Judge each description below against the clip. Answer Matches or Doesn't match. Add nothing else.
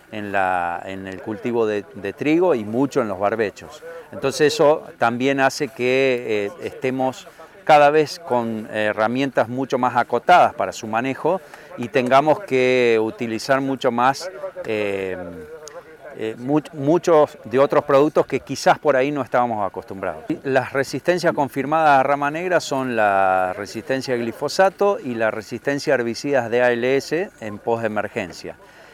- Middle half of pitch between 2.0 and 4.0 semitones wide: Doesn't match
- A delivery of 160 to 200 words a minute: Doesn't match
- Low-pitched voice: Matches